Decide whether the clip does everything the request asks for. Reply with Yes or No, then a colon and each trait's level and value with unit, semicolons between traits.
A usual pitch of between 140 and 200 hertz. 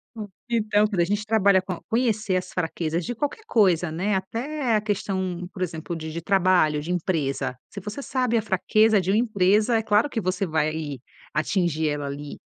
Yes: high, 190 Hz